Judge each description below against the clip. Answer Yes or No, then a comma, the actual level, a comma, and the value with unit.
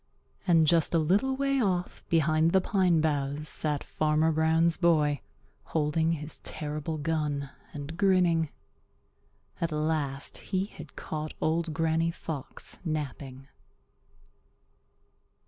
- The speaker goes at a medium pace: No, slow, 110 wpm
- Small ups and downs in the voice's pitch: Yes, narrow, 2.0 semitones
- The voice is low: No, medium, 160 Hz